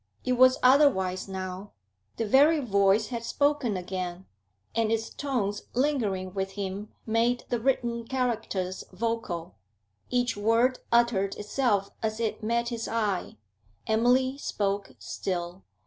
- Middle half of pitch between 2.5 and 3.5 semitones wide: No, average, 4.0 semitones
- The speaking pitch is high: Yes, high, 225 Hz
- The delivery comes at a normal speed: No, slow, 125 wpm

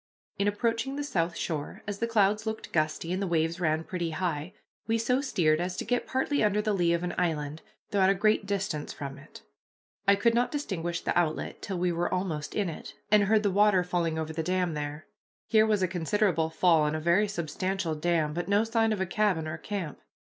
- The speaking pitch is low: No, medium, 180 Hz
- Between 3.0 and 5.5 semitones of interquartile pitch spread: Yes, average, 4.4 semitones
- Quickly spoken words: Yes, fast, 220 wpm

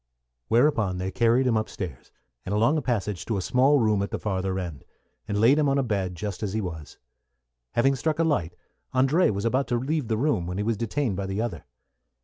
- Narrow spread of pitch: No, wide, 5.4 semitones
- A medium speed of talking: No, fast, 225 wpm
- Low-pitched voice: Yes, low, 110 Hz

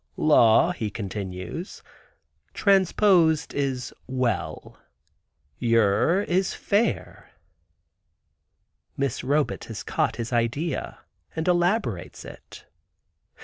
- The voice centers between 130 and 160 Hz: Yes, medium, 140 Hz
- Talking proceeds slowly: Yes, slow, 80 wpm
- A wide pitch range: Yes, wide, 7.3 semitones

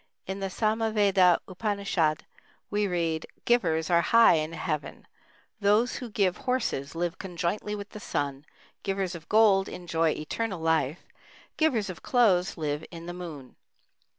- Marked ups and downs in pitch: No, average, 4.3 semitones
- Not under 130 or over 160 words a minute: Yes, average, 140 wpm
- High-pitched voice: No, medium, 180 Hz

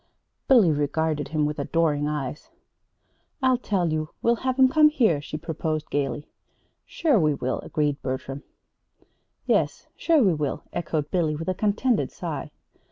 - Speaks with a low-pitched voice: No, medium, 160 Hz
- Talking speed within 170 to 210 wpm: No, average, 150 wpm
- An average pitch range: No, wide, 6.6 semitones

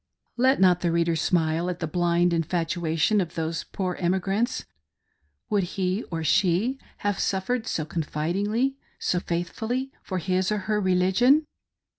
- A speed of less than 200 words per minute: Yes, average, 150 wpm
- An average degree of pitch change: Yes, average, 3.6 semitones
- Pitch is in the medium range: Yes, medium, 180 Hz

